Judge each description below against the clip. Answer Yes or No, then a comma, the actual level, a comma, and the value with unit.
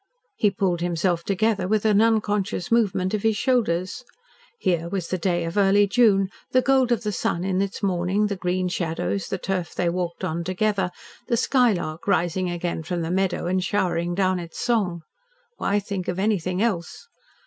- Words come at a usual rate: Yes, average, 180 wpm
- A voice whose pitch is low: No, high, 190 Hz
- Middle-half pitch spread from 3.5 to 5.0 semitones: No, average, 3.0 semitones